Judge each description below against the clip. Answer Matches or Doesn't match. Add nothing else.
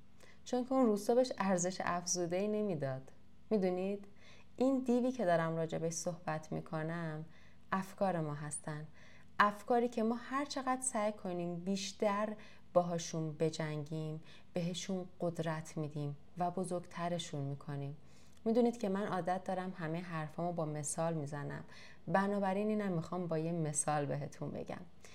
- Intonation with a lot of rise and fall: Doesn't match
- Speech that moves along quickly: Doesn't match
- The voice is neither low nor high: Matches